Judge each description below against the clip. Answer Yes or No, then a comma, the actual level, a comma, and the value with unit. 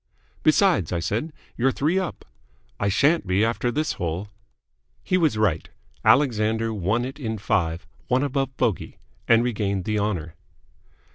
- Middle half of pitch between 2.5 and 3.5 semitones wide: No, average, 5.3 semitones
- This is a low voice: Yes, low, 110 Hz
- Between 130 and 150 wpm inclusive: Yes, average, 145 wpm